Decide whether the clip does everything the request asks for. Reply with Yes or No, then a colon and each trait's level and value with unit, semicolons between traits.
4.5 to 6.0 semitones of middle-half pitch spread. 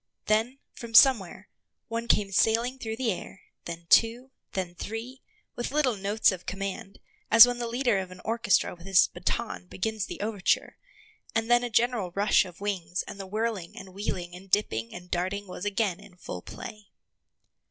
No: average, 3.7 semitones